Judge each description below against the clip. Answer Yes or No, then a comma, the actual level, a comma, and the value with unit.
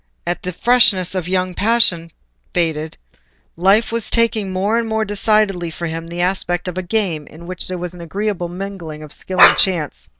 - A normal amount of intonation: Yes, average, 3.3 semitones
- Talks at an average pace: Yes, average, 190 wpm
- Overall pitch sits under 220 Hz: Yes, medium, 185 Hz